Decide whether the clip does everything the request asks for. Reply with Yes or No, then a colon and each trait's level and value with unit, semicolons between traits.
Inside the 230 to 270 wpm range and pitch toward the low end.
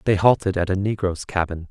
No: fast, 210 wpm; very low, 95 Hz